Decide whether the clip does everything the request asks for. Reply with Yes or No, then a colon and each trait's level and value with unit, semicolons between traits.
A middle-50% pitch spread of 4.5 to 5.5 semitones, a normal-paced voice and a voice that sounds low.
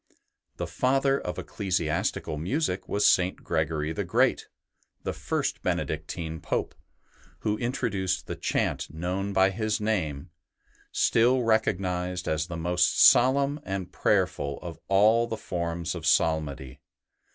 No: average, 5.1 semitones; slow, 125 wpm; very low, 90 Hz